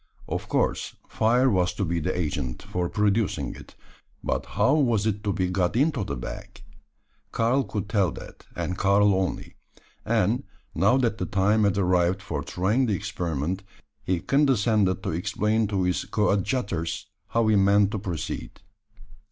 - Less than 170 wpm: Yes, average, 160 wpm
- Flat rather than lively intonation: No, average, 3.3 semitones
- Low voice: Yes, low, 100 Hz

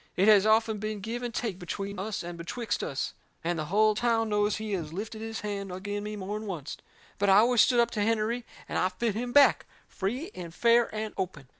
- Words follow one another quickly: Yes, fast, 225 wpm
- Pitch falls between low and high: No, high, 210 Hz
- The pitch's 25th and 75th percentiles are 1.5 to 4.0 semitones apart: Yes, average, 2.9 semitones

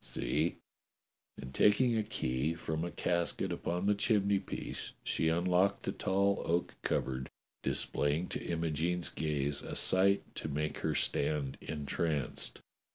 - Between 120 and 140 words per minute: Yes, slow, 135 wpm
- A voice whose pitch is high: No, very low, 85 Hz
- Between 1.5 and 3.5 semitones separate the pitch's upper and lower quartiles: No, average, 4.4 semitones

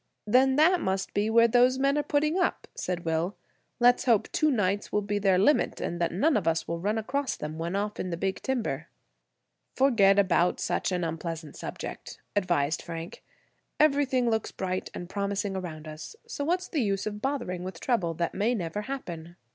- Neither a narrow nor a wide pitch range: No, wide, 6.5 semitones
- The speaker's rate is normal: Yes, average, 185 wpm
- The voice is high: Yes, high, 200 Hz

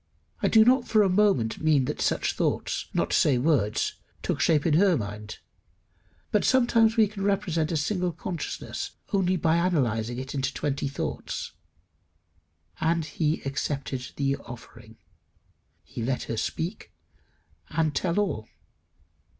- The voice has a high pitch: No, medium, 155 Hz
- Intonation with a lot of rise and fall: Yes, wide, 6.2 semitones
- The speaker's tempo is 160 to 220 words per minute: No, average, 140 wpm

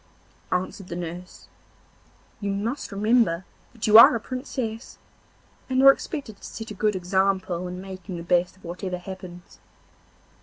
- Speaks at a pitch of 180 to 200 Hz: Yes, high, 190 Hz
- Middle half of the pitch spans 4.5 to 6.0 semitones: No, average, 3.7 semitones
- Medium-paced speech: Yes, average, 150 wpm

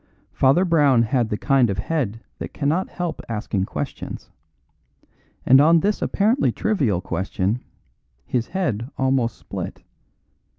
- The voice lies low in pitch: Yes, low, 130 Hz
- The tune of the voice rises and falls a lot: Yes, wide, 6.5 semitones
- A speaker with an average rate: No, slow, 125 wpm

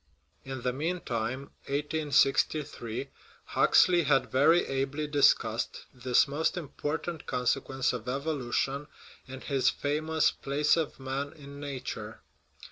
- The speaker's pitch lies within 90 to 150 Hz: Yes, medium, 140 Hz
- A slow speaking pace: Yes, slow, 115 wpm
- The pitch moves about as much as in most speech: No, narrow, 2.3 semitones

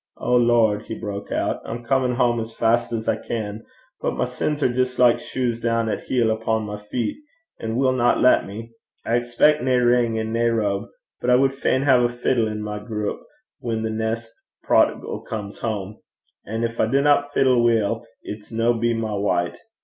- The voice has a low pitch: Yes, low, 115 Hz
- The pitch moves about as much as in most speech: No, narrow, 1.9 semitones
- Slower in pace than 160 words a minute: No, fast, 205 wpm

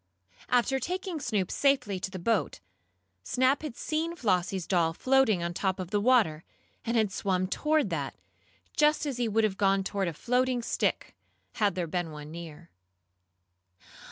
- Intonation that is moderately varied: No, wide, 6.0 semitones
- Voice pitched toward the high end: Yes, high, 210 Hz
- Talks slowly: No, average, 165 wpm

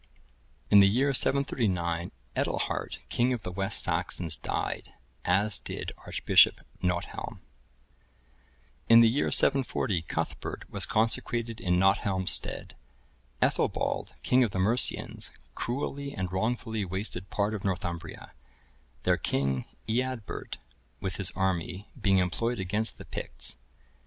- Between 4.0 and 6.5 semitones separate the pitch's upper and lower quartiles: Yes, average, 4.3 semitones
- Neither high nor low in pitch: No, low, 100 Hz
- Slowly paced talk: Yes, slow, 120 wpm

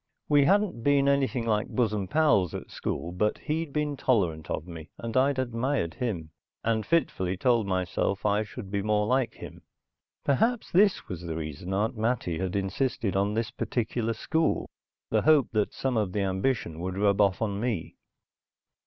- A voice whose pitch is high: No, low, 110 Hz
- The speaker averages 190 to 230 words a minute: No, average, 170 wpm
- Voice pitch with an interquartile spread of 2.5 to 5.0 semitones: No, wide, 5.6 semitones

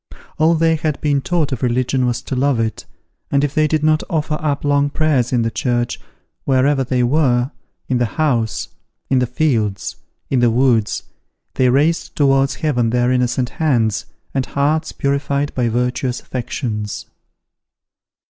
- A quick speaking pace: No, average, 155 wpm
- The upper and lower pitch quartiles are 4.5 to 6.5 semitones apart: No, average, 3.2 semitones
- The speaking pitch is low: Yes, low, 130 Hz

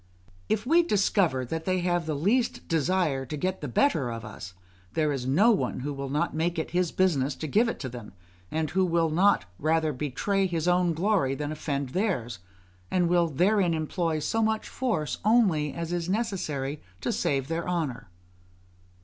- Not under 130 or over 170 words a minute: No, average, 180 wpm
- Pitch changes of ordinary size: Yes, average, 4.8 semitones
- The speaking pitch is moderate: Yes, medium, 165 Hz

